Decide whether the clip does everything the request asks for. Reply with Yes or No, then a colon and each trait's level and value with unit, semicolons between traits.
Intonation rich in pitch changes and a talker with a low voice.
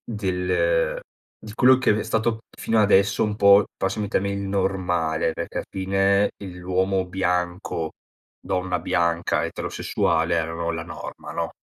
No: average, 2.9 semitones; very low, 95 Hz